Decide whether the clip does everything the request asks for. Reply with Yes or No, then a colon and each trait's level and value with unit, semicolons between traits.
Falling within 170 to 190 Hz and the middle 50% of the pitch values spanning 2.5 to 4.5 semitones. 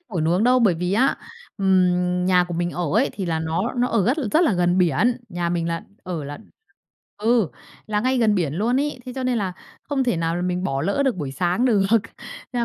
No: medium, 185 Hz; wide, 5.5 semitones